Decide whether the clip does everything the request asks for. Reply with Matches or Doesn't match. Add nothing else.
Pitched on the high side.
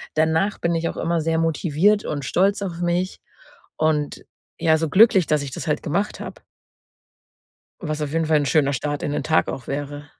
Doesn't match